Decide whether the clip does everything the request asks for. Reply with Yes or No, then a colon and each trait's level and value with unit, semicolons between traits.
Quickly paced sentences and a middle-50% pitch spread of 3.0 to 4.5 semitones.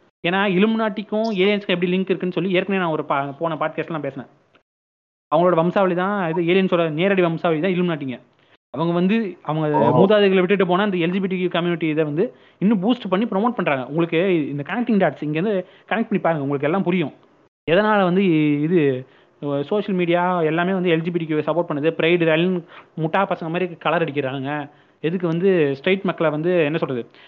Yes: fast, 165 wpm; average, 3.4 semitones